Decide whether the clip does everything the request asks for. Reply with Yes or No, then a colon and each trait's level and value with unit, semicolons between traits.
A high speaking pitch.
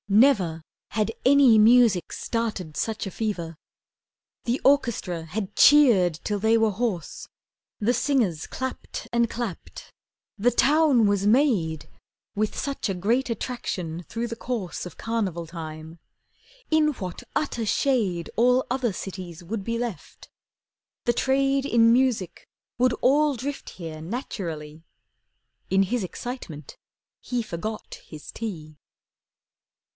Yes: high, 220 Hz